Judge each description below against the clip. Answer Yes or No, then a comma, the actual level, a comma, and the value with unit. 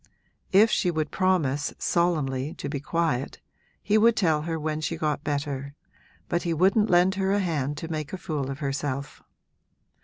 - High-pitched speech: No, medium, 155 Hz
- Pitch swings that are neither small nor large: Yes, average, 3.9 semitones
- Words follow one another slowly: No, average, 175 wpm